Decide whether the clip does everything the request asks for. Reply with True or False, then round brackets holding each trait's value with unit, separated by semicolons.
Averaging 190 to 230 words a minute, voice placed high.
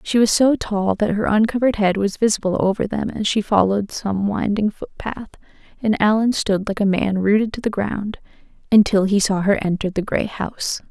True (200 wpm; 205 Hz)